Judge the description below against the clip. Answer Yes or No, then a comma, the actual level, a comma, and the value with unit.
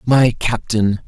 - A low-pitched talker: Yes, low, 115 Hz